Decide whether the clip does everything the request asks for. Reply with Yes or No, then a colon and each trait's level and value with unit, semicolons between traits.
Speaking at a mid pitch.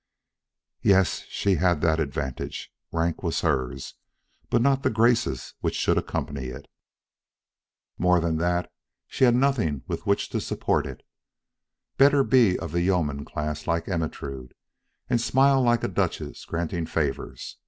No: very low, 85 Hz